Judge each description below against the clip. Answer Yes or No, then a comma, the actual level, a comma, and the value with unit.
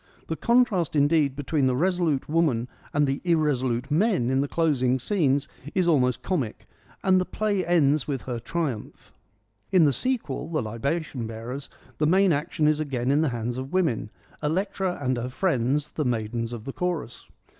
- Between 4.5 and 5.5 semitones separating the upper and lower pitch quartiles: Yes, average, 5.0 semitones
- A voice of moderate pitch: Yes, medium, 145 Hz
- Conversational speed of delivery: Yes, average, 170 wpm